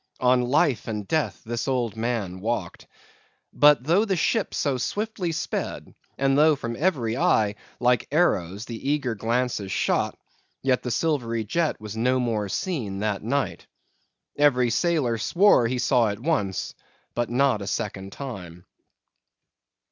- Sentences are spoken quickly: No, average, 145 wpm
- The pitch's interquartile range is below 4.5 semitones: No, average, 5.0 semitones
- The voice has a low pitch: Yes, low, 125 Hz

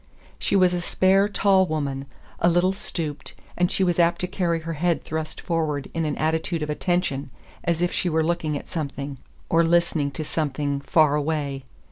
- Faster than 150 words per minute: Yes, average, 185 wpm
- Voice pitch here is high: No, medium, 160 Hz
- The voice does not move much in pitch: No, average, 3.0 semitones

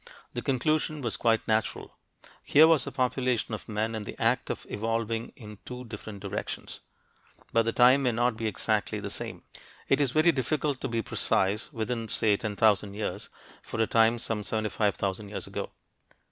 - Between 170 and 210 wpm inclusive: Yes, average, 175 wpm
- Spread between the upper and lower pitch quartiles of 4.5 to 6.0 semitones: No, average, 2.9 semitones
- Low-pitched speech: Yes, low, 115 Hz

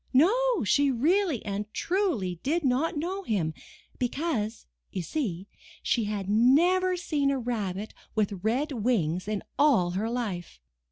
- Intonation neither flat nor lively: No, wide, 7.2 semitones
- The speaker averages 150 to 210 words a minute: No, slow, 135 wpm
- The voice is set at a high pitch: Yes, high, 245 Hz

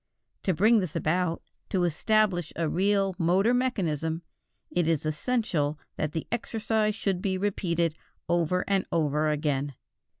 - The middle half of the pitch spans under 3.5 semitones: No, average, 4.3 semitones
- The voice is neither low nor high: Yes, medium, 175 Hz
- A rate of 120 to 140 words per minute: Yes, slow, 135 wpm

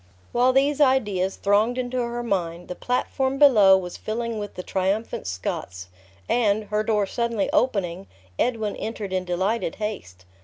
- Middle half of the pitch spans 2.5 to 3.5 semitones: No, average, 4.2 semitones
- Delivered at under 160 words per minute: Yes, average, 150 wpm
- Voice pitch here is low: No, high, 210 Hz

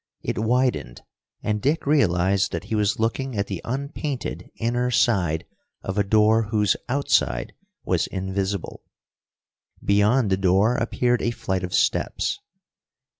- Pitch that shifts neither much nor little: Yes, average, 4.3 semitones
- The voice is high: No, low, 105 Hz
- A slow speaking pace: Yes, slow, 130 wpm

